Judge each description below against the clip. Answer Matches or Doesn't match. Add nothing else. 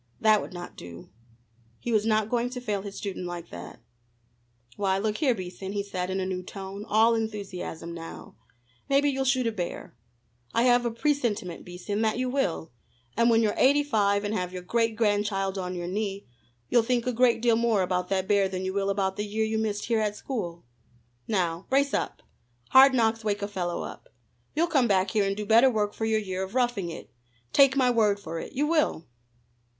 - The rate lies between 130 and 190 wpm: Doesn't match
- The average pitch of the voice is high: Matches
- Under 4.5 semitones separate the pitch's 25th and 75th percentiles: Matches